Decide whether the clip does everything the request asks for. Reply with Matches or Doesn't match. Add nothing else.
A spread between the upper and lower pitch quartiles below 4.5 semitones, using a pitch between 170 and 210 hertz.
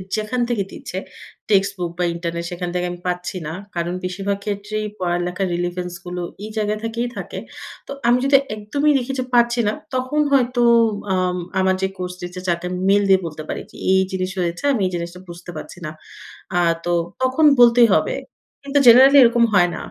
Doesn't match